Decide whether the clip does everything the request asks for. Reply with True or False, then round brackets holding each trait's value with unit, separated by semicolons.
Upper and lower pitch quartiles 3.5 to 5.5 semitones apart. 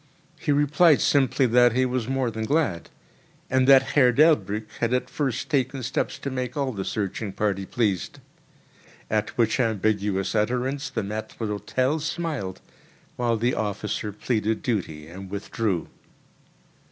True (4.1 semitones)